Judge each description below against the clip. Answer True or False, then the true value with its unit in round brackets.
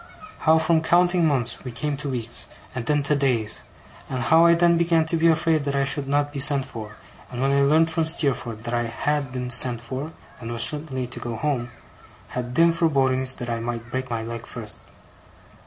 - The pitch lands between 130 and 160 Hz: True (135 Hz)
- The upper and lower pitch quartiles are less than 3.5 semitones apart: False (4.7 semitones)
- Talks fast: True (210 wpm)